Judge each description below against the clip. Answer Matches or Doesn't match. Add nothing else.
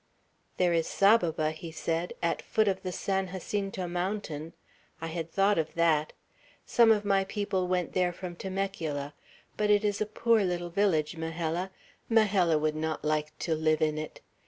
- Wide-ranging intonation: Doesn't match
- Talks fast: Doesn't match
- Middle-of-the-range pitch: Matches